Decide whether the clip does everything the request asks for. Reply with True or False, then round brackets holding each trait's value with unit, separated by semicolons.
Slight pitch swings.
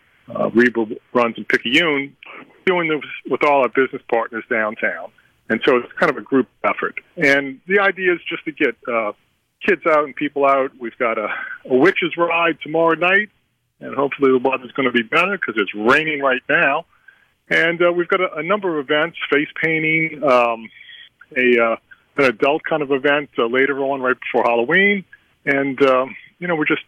False (4.3 semitones)